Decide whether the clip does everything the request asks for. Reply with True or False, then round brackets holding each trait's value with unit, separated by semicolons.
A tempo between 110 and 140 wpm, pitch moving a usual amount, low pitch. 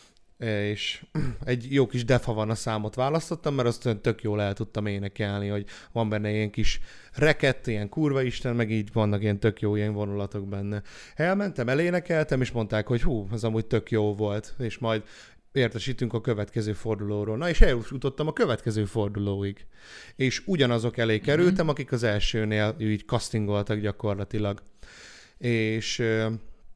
False (150 wpm; 3.2 semitones; 110 Hz)